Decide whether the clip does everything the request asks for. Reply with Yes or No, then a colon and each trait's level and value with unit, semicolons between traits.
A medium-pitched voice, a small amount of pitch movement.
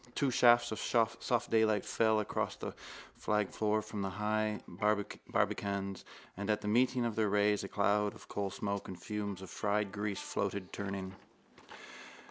No: low, 105 Hz; narrow, 1.5 semitones